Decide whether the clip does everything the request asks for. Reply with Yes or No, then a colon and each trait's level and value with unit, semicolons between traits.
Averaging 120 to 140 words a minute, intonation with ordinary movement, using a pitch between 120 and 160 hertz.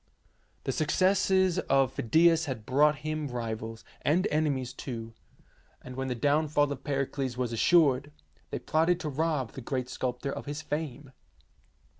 No: average, 150 wpm; average, 3.5 semitones; medium, 140 Hz